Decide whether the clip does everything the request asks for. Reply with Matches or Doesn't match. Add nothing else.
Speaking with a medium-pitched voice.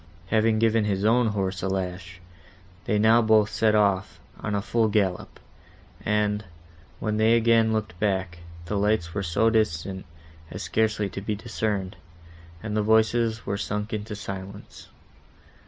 Doesn't match